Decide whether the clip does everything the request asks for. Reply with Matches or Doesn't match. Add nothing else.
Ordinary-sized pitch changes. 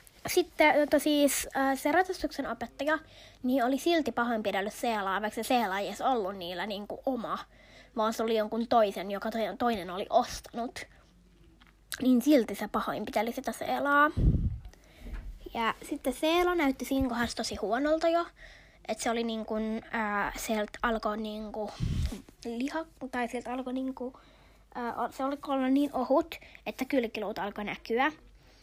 Matches